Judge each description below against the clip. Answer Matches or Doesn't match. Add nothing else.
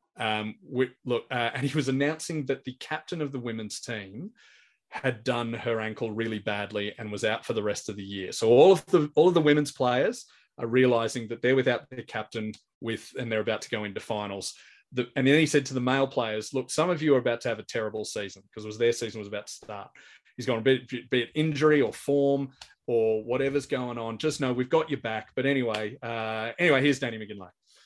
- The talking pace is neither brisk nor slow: Doesn't match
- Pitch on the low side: Matches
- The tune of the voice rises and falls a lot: Doesn't match